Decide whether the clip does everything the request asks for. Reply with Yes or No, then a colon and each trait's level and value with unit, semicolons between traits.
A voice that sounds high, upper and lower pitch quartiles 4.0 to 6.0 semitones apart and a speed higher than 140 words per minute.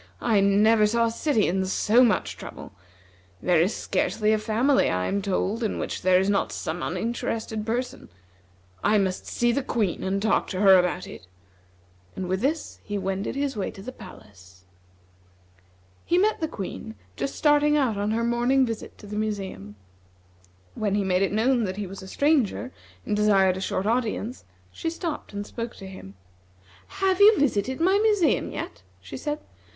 Yes: high, 215 Hz; average, 4.8 semitones; average, 180 wpm